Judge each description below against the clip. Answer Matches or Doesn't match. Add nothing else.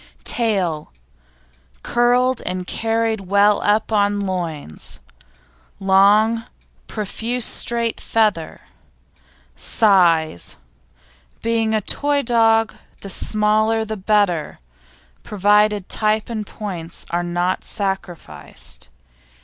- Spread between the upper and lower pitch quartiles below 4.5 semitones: Matches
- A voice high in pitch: Matches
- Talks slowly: Matches